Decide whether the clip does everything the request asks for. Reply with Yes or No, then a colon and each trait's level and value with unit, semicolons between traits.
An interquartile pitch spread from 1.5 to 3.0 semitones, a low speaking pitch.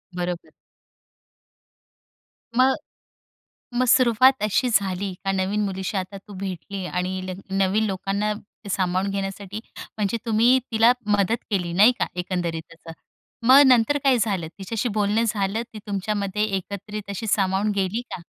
No: average, 2.7 semitones; high, 200 Hz